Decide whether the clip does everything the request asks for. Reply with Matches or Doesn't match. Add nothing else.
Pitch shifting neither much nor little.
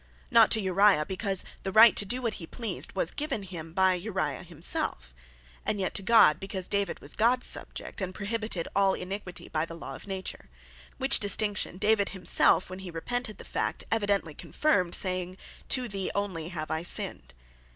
Matches